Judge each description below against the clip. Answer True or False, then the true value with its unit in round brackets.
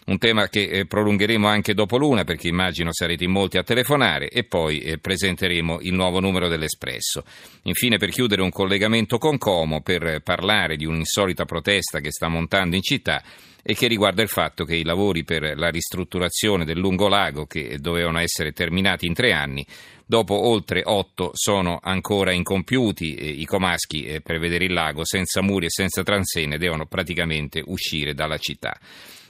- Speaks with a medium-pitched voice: False (90 Hz)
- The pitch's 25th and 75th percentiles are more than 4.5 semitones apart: False (3.5 semitones)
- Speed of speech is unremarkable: False (175 wpm)